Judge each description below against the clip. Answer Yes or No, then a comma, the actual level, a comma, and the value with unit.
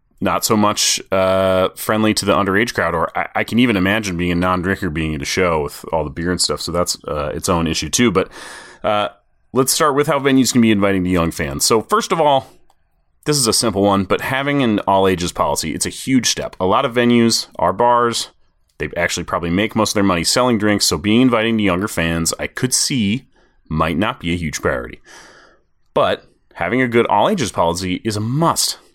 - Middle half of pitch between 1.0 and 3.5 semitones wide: No, average, 4.7 semitones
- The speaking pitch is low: Yes, low, 100 Hz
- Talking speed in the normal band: No, fast, 225 wpm